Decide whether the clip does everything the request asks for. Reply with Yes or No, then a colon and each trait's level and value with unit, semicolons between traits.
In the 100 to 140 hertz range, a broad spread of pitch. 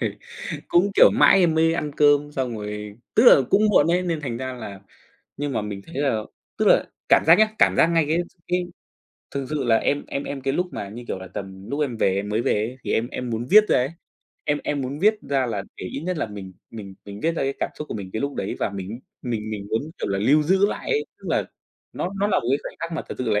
Yes: low, 135 Hz; wide, 7.2 semitones